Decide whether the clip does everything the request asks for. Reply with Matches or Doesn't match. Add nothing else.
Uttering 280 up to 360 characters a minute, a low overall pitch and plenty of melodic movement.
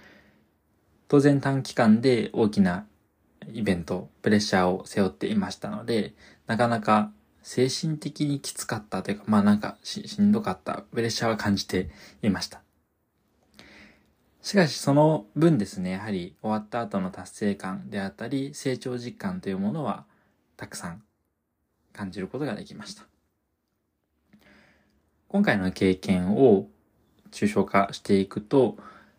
Matches